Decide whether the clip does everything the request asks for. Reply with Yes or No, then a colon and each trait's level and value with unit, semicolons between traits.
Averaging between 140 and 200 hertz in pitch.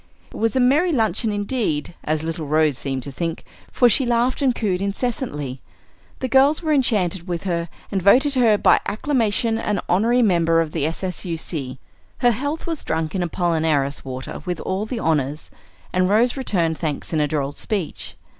Yes: medium, 185 Hz